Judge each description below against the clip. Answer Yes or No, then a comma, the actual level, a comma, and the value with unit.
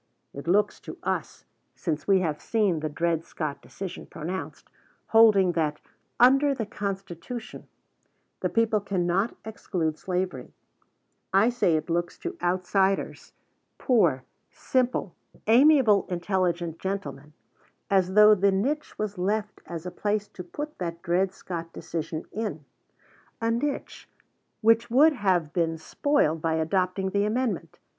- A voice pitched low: No, high, 190 Hz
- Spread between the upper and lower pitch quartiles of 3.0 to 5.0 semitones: Yes, average, 4.5 semitones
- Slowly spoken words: Yes, slow, 130 wpm